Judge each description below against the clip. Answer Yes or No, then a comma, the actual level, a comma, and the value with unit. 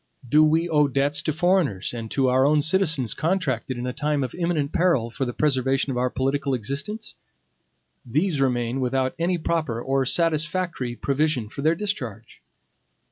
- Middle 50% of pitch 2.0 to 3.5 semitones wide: No, average, 4.2 semitones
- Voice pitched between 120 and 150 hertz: Yes, medium, 140 Hz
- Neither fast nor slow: Yes, average, 165 wpm